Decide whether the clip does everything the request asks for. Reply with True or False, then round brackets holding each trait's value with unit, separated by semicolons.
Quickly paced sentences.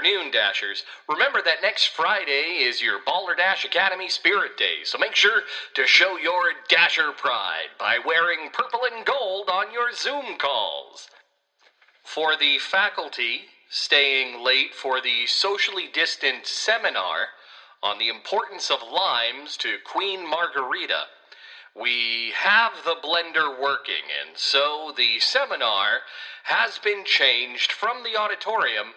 False (135 wpm)